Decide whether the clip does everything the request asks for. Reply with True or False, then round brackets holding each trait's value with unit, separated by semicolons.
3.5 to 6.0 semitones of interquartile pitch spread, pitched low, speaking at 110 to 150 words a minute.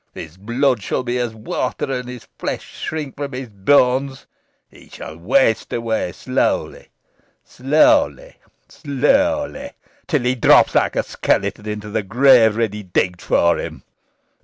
True (4.8 semitones; 125 Hz; 135 wpm)